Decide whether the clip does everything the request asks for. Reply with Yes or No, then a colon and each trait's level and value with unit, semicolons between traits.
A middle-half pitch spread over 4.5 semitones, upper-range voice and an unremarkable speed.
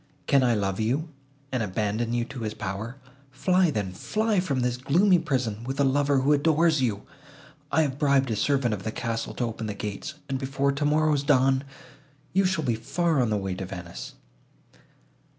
No: average, 4.9 semitones; low, 130 Hz; average, 185 wpm